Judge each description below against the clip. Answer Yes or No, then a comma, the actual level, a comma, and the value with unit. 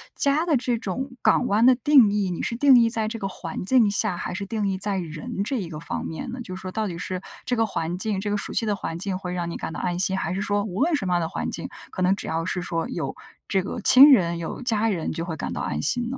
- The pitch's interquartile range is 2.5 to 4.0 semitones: No, average, 4.4 semitones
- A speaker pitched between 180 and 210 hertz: Yes, high, 200 Hz